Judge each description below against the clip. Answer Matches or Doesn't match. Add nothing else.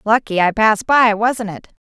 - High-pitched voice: Matches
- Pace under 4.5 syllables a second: Doesn't match